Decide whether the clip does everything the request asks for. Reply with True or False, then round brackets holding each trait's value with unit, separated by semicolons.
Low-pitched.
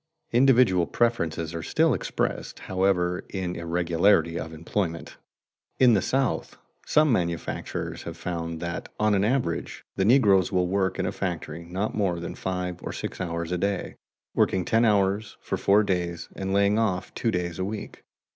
True (95 Hz)